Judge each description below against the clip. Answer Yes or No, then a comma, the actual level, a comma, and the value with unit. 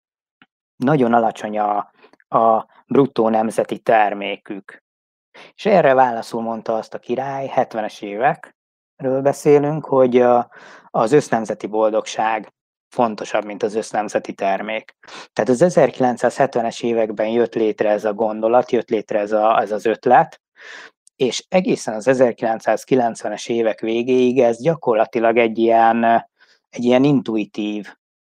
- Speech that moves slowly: No, average, 115 wpm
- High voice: No, low, 115 Hz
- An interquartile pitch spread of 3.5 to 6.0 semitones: No, narrow, 2.6 semitones